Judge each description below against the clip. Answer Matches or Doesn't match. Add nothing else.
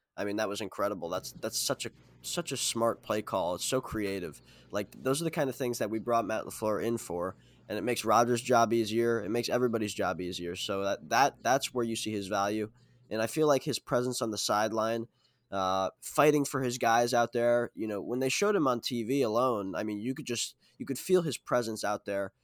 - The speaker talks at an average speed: Doesn't match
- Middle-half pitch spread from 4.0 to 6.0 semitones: Doesn't match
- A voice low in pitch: Matches